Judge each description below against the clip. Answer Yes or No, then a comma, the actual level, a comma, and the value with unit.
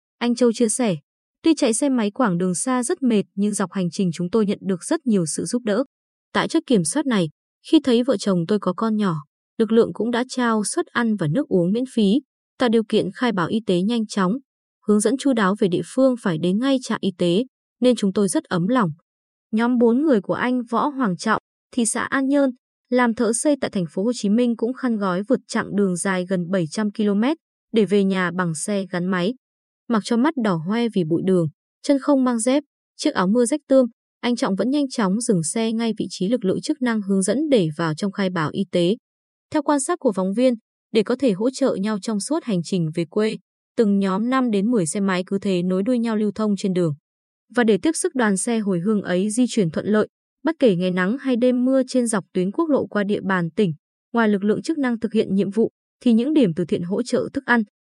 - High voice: Yes, high, 220 Hz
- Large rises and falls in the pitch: No, average, 4.6 semitones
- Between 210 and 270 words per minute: Yes, average, 245 wpm